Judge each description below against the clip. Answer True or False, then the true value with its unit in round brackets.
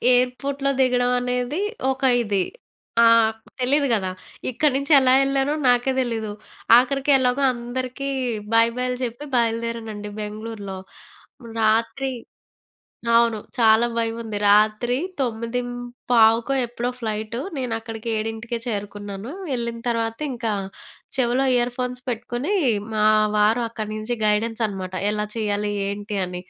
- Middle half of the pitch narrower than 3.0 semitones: True (2.5 semitones)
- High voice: True (235 Hz)